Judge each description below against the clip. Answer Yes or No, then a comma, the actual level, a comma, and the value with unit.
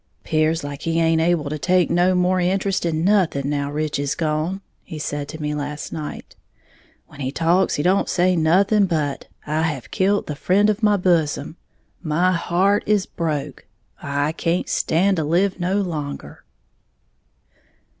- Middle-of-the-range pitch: Yes, medium, 165 Hz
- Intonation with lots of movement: No, average, 3.7 semitones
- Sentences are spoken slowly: No, average, 165 wpm